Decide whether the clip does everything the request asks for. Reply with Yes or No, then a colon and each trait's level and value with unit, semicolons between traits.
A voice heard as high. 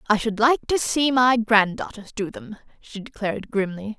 Yes: high, 220 Hz